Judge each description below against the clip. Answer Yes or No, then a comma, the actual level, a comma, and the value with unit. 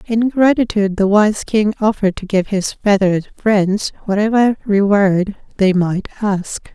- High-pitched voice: Yes, high, 205 Hz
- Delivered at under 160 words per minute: Yes, average, 140 wpm